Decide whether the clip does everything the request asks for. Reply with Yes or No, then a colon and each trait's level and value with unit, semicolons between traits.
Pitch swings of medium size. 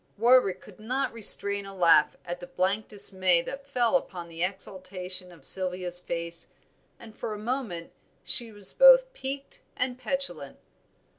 No: wide, 5.7 semitones